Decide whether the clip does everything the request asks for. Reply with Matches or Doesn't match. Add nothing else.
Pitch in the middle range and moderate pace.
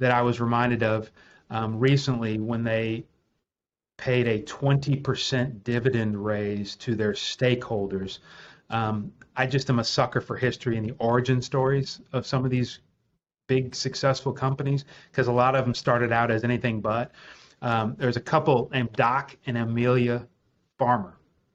Doesn't match